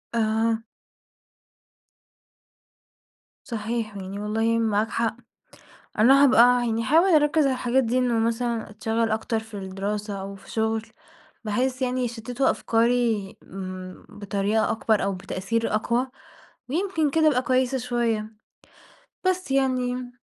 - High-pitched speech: Yes, high, 230 Hz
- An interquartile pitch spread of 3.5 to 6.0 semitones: No, average, 2.8 semitones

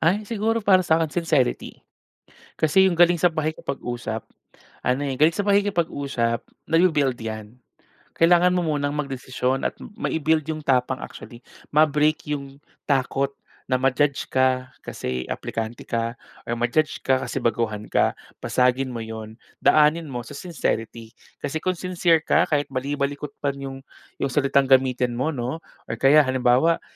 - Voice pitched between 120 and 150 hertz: Yes, medium, 140 Hz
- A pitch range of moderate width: Yes, average, 4.1 semitones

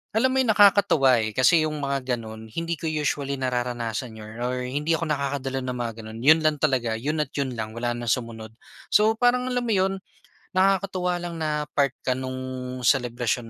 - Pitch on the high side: No, low, 135 Hz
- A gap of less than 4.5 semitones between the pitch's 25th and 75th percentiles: No, wide, 5.6 semitones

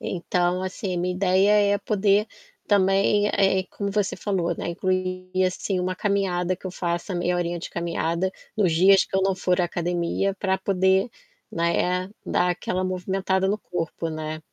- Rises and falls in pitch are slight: Yes, narrow, 1.6 semitones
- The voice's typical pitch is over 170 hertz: Yes, medium, 185 Hz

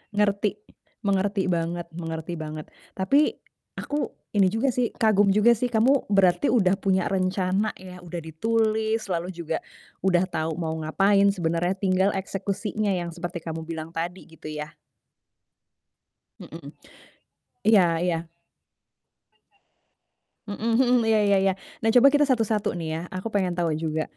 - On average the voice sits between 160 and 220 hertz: Yes, high, 190 Hz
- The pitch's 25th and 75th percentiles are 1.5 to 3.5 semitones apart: No, average, 4.1 semitones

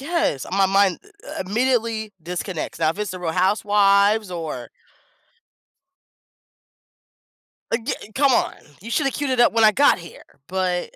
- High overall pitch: Yes, high, 200 Hz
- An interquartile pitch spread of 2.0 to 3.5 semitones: No, average, 4.4 semitones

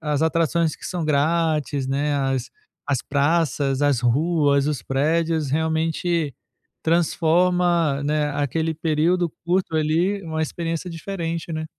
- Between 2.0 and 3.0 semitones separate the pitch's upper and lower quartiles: Yes, narrow, 2.6 semitones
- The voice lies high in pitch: No, medium, 160 Hz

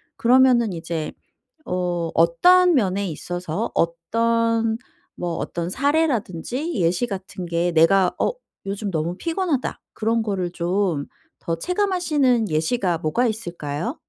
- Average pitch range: No, wide, 6.2 semitones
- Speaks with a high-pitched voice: Yes, high, 195 Hz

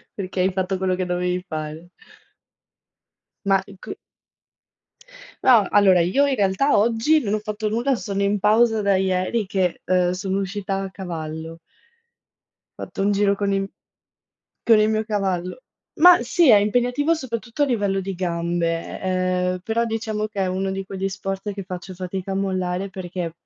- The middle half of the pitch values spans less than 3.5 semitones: Yes, average, 2.7 semitones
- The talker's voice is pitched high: Yes, high, 195 Hz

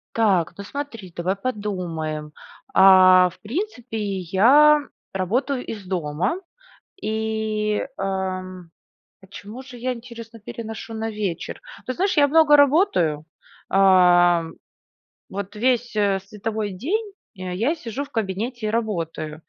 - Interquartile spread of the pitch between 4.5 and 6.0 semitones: Yes, average, 4.8 semitones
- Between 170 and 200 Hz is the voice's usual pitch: No, high, 210 Hz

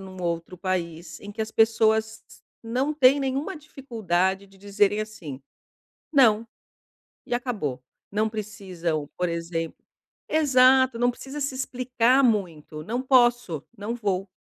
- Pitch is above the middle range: Yes, high, 215 Hz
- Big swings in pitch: Yes, wide, 5.7 semitones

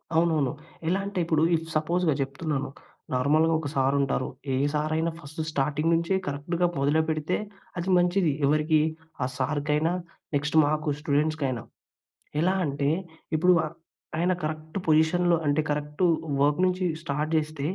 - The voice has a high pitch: No, medium, 155 Hz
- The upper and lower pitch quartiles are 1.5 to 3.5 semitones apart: Yes, narrow, 2.6 semitones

